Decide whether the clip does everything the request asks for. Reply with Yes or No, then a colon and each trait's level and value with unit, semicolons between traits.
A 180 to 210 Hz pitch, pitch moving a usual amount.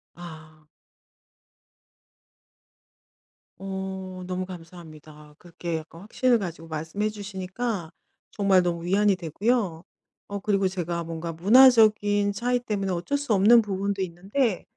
Yes: high, 190 Hz; average, 3.4 semitones